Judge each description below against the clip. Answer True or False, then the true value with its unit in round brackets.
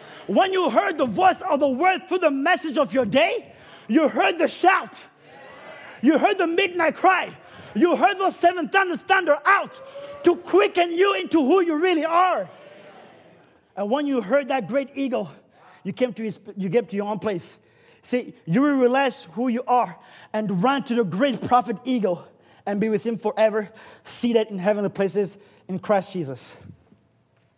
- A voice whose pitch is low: False (265 Hz)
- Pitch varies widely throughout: True (8.4 semitones)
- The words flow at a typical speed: True (175 wpm)